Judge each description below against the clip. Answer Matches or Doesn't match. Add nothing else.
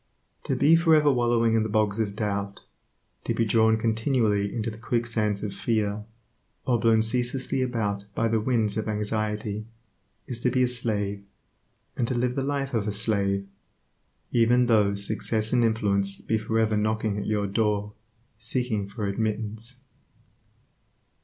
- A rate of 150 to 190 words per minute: Matches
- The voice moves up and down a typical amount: Doesn't match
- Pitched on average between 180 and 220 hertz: Doesn't match